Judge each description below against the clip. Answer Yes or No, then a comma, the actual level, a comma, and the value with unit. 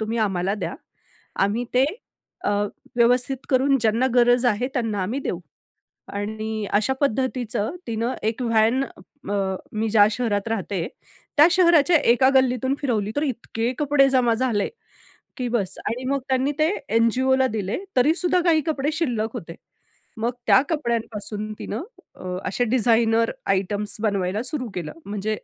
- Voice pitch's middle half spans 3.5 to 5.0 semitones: Yes, average, 3.8 semitones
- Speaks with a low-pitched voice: No, high, 230 Hz